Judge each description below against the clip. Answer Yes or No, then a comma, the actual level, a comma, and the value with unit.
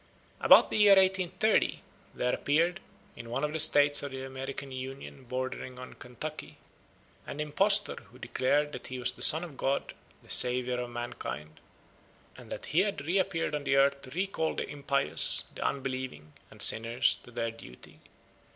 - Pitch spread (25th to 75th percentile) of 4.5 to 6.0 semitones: No, average, 3.7 semitones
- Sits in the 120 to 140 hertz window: Yes, low, 135 Hz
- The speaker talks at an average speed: Yes, average, 165 wpm